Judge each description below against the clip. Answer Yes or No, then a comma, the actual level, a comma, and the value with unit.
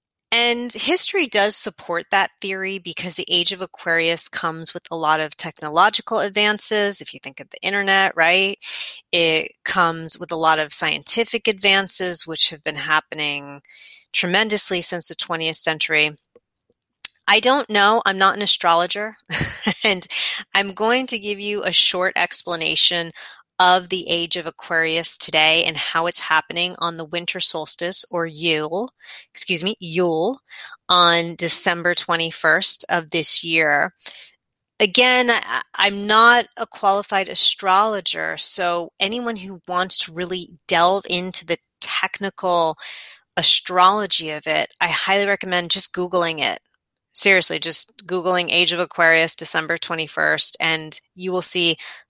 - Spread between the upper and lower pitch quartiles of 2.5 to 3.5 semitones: Yes, average, 3.2 semitones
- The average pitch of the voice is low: No, medium, 180 Hz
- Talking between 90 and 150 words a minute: Yes, average, 140 wpm